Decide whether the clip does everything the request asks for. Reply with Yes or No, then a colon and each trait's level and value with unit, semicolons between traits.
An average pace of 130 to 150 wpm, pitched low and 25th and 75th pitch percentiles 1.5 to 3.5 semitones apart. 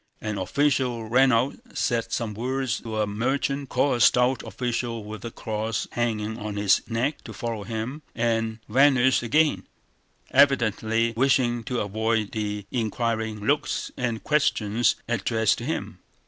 Yes: average, 145 wpm; low, 115 Hz; average, 2.7 semitones